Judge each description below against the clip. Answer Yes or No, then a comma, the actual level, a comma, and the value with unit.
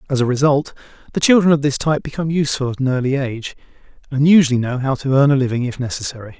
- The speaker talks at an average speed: No, fast, 225 wpm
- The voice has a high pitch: No, low, 135 Hz